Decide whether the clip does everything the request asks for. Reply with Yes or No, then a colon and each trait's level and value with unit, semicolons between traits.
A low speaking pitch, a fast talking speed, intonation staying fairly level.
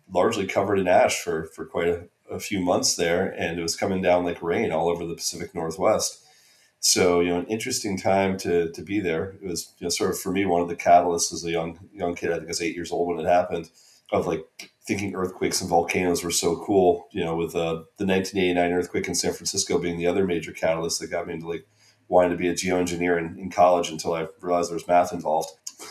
Yes: very low, 85 Hz; fast, 245 wpm; narrow, 1.2 semitones